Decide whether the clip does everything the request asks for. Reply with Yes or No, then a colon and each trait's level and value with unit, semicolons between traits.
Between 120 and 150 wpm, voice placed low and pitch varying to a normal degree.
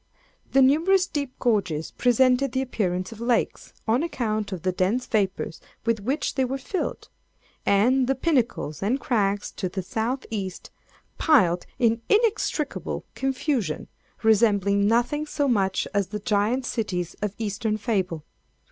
No: average, 140 wpm; high, 225 Hz; average, 4.8 semitones